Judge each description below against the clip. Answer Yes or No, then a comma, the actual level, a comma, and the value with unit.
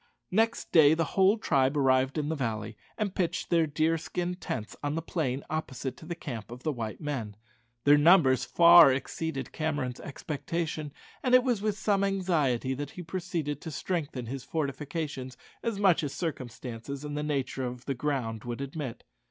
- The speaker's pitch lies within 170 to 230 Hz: No, medium, 150 Hz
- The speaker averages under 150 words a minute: No, average, 175 wpm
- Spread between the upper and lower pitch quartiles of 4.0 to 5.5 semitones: Yes, average, 4.4 semitones